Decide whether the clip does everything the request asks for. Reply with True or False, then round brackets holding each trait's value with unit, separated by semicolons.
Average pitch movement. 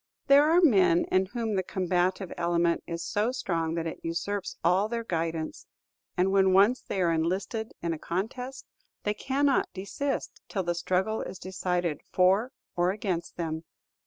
True (4.2 semitones)